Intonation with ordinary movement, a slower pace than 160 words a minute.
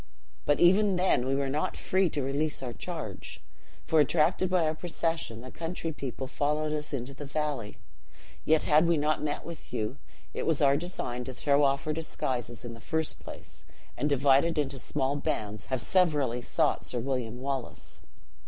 No: average, 3.5 semitones; average, 180 wpm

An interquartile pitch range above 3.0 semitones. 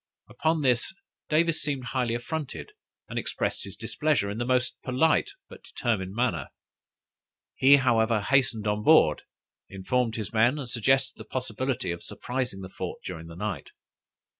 Yes: average, 4.1 semitones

